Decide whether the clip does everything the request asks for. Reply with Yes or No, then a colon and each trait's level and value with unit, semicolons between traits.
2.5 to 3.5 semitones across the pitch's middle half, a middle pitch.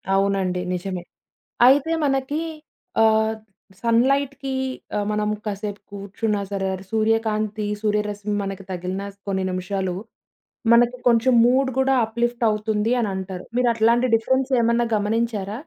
No: average, 3.1 semitones; high, 215 Hz